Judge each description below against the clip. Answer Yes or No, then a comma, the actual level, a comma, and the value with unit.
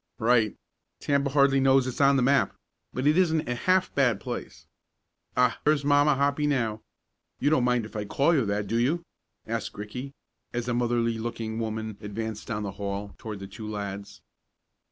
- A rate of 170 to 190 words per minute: Yes, average, 180 wpm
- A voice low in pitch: Yes, low, 120 Hz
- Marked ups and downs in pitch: No, average, 4.3 semitones